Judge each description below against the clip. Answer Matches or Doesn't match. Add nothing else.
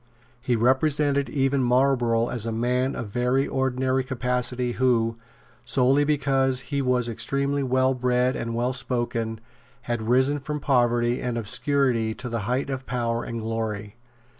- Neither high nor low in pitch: Doesn't match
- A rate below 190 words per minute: Matches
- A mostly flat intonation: Matches